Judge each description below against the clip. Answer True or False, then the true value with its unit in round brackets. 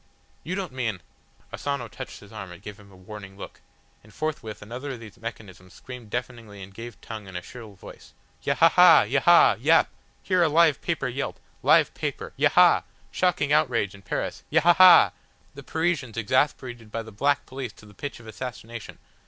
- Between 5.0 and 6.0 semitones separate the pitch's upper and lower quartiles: True (5.3 semitones)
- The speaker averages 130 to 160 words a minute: False (175 wpm)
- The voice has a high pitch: False (115 Hz)